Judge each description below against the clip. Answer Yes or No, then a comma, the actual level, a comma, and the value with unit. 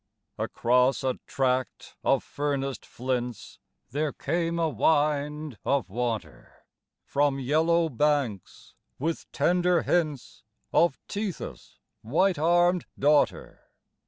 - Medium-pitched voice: Yes, medium, 145 Hz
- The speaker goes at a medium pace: No, slow, 100 wpm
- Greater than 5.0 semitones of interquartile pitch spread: No, average, 4.4 semitones